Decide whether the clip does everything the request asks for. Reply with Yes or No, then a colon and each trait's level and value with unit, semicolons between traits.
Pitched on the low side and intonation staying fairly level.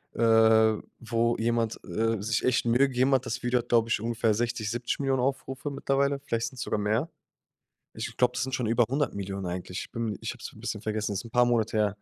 Yes: low, 115 Hz; narrow, 2.3 semitones